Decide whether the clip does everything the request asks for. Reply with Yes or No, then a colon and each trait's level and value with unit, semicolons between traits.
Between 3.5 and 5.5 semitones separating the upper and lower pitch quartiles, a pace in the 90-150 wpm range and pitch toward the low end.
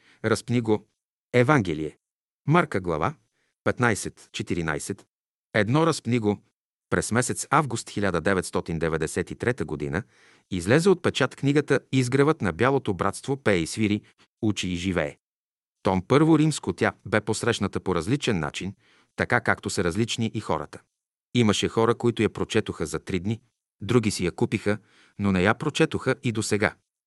Yes: average, 4.2 semitones; average, 140 wpm; low, 110 Hz